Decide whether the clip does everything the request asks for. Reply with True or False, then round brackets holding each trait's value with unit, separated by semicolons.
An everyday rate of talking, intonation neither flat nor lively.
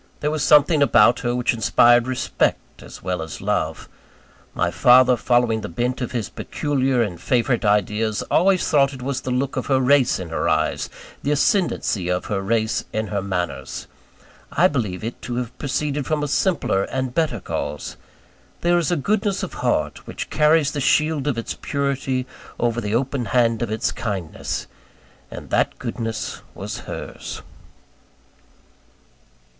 True (165 wpm; 4.4 semitones)